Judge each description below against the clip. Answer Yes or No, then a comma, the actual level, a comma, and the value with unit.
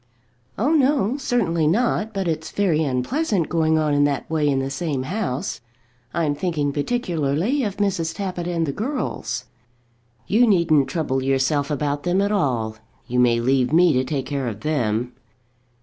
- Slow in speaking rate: No, average, 165 wpm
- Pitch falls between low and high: Yes, medium, 155 Hz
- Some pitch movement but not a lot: No, wide, 6.2 semitones